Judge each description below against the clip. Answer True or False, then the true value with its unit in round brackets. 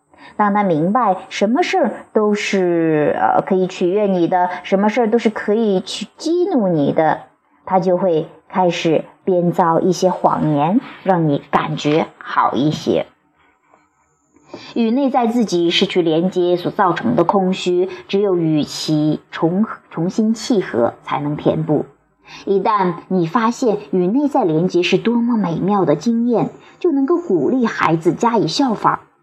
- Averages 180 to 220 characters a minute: True (215 characters per minute)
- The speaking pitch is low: False (190 Hz)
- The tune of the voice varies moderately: True (4.6 semitones)